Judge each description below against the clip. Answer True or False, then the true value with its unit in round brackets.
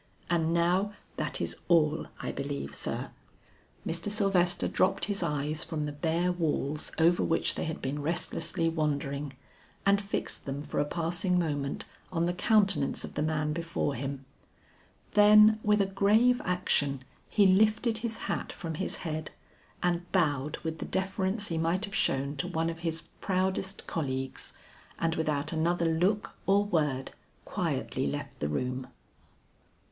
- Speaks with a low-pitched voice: False (165 Hz)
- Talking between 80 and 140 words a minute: False (150 wpm)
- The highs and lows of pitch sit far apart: False (4.3 semitones)